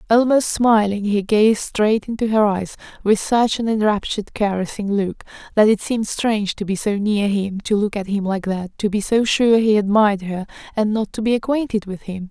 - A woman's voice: Yes, female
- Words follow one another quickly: Yes, fast, 210 wpm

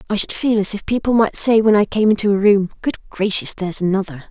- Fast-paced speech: Yes, fast, 250 wpm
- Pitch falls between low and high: No, high, 205 Hz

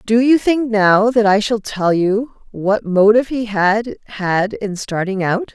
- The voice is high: Yes, high, 215 Hz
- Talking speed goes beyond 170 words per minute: Yes, average, 185 wpm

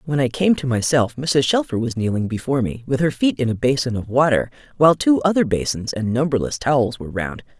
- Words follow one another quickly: Yes, fast, 220 wpm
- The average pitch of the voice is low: Yes, low, 130 Hz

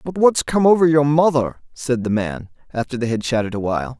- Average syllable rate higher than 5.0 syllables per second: Yes, 5.9 syllables/s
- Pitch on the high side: No, low, 130 Hz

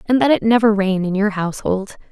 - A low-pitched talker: No, high, 210 Hz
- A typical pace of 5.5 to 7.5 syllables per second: Yes, 5.9 syllables/s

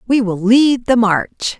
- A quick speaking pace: No, average, 190 wpm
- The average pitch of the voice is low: No, high, 230 Hz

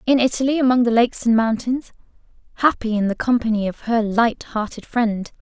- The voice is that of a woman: Yes, female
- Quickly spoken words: No, average, 175 wpm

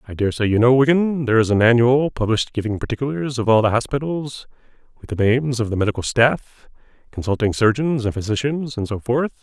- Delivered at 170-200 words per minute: Yes, average, 190 wpm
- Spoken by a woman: No, male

